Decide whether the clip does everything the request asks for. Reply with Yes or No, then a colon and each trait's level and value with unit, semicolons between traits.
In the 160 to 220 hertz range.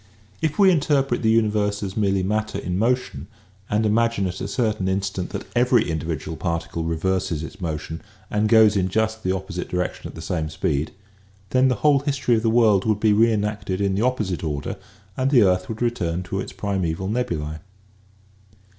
No: low, 100 Hz